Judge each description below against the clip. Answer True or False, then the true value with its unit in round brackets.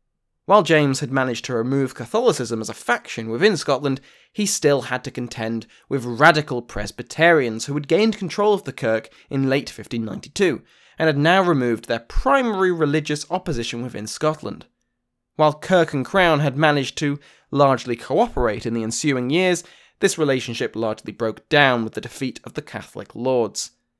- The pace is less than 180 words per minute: True (165 wpm)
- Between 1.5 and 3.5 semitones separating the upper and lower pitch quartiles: False (5.0 semitones)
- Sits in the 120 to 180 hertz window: True (135 Hz)